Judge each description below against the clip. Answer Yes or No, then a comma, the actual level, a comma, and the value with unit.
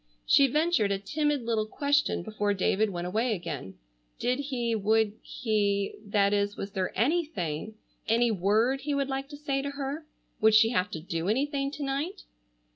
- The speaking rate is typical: Yes, average, 170 wpm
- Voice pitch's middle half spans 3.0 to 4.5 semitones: No, wide, 5.5 semitones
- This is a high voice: Yes, high, 225 Hz